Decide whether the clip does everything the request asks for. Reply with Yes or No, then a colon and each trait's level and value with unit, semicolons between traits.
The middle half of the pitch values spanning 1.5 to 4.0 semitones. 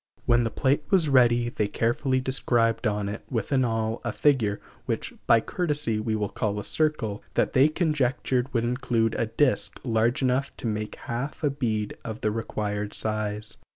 Yes: average, 3.4 semitones